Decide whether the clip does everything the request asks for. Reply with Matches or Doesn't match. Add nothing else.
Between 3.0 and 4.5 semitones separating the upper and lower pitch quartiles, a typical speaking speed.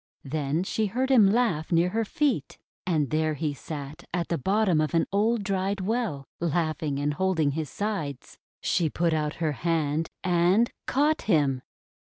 Doesn't match